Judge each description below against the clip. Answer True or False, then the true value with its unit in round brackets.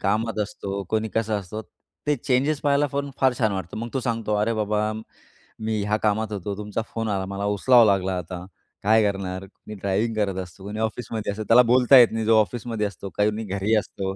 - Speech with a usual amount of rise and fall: False (2.3 semitones)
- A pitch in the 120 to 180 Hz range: False (105 Hz)